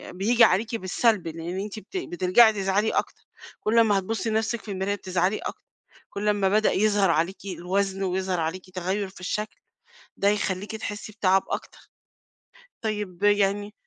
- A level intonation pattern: Yes, narrow, 2.3 semitones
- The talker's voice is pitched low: No, high, 200 Hz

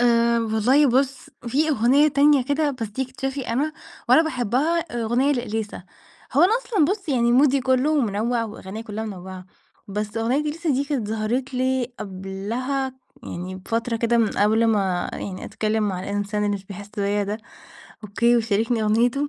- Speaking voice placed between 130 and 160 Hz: No, high, 235 Hz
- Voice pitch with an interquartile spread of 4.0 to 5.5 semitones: Yes, average, 4.3 semitones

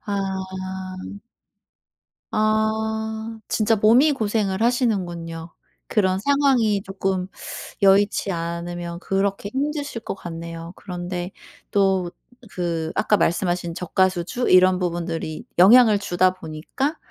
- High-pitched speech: Yes, high, 195 Hz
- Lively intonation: No, average, 3.9 semitones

